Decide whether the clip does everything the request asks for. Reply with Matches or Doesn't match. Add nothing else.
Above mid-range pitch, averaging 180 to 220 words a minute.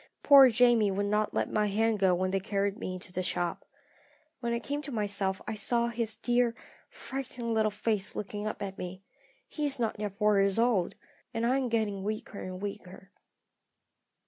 Matches